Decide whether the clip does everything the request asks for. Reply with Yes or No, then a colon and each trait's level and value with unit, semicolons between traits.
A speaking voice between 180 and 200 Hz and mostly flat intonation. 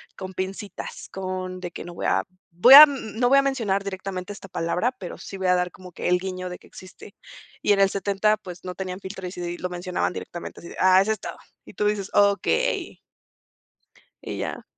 Yes: high, 190 Hz; narrow, 2.1 semitones